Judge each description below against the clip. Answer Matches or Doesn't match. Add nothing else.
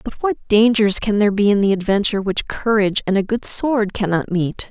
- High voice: Matches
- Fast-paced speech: Matches